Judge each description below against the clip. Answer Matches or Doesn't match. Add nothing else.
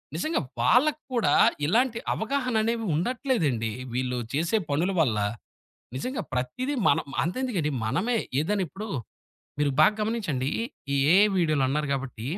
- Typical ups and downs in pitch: Doesn't match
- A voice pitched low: Doesn't match